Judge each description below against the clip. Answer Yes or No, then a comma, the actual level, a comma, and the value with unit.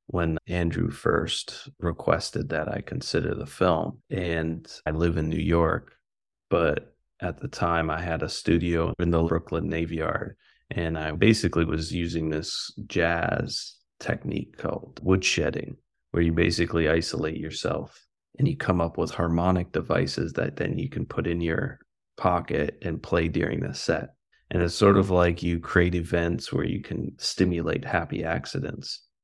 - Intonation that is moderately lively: No, narrow, 1.0 semitones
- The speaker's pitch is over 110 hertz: No, very low, 85 Hz